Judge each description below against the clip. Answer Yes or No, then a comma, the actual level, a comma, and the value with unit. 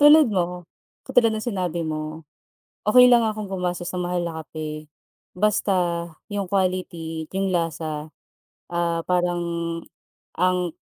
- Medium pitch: Yes, medium, 180 Hz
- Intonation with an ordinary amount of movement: Yes, average, 3.2 semitones